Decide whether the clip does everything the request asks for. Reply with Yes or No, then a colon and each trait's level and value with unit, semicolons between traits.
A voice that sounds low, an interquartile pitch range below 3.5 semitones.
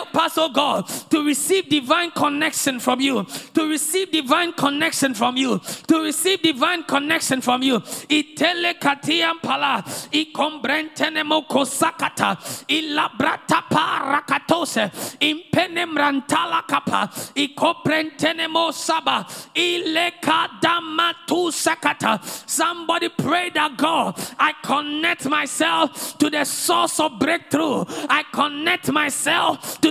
No: very high, 310 Hz; narrow, 2.4 semitones